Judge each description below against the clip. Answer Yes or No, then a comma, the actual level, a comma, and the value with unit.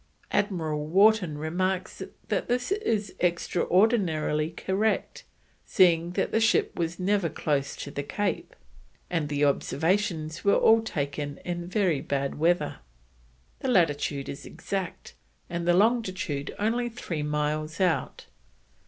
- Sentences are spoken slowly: Yes, slow, 125 wpm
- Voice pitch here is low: No, medium, 175 Hz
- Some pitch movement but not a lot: Yes, average, 5.0 semitones